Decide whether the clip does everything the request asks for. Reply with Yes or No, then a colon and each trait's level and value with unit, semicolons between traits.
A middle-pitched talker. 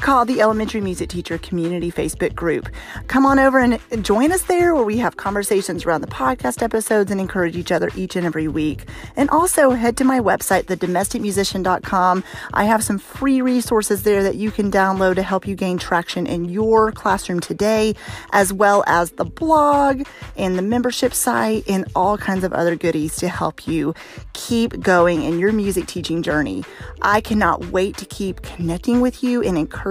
No: high, 200 Hz